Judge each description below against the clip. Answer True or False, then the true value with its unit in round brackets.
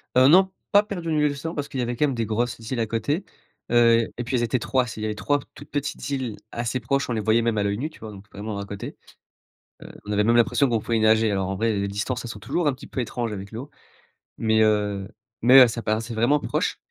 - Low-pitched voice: True (115 Hz)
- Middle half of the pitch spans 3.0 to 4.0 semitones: True (3.7 semitones)